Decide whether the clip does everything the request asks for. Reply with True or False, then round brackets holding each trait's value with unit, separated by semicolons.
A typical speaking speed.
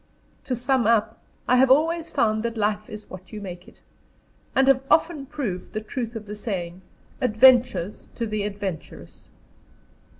True (160 wpm)